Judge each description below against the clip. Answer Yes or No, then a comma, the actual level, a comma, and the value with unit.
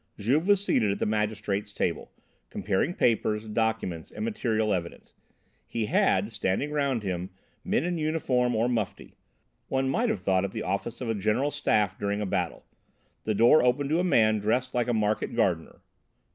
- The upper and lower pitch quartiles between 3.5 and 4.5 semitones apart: Yes, average, 4.1 semitones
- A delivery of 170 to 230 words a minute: Yes, average, 175 wpm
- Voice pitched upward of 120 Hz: No, low, 110 Hz